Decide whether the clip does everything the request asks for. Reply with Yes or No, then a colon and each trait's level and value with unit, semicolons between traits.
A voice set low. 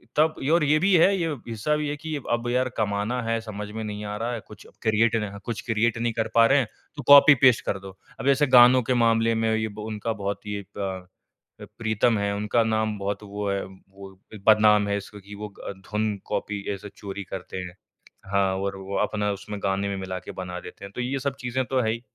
Yes: low, 110 Hz